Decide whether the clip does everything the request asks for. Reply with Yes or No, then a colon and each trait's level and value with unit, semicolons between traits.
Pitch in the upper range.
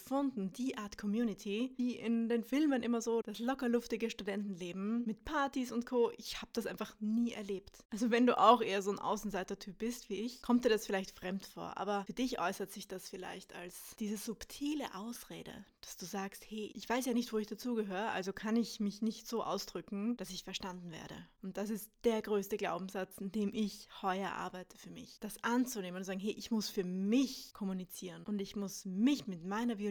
Yes: high, 215 Hz